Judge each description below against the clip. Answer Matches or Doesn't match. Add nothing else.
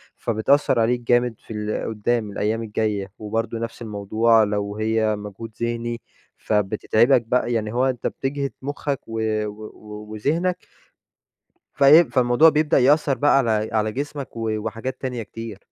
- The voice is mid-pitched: Doesn't match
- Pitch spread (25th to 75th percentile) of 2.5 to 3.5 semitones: Matches